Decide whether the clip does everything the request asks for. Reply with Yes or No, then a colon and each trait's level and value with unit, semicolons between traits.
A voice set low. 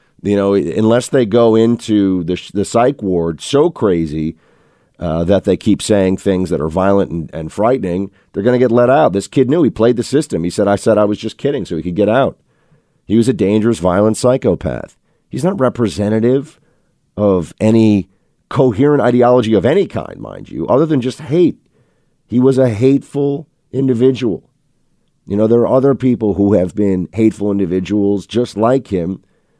Yes: low, 110 Hz